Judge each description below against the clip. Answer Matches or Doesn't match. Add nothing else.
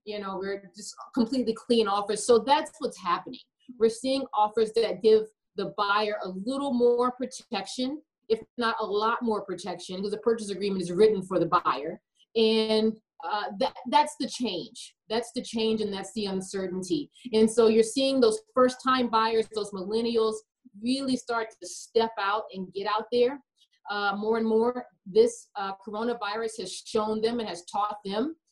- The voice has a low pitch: Doesn't match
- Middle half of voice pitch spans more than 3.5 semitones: Doesn't match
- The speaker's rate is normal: Matches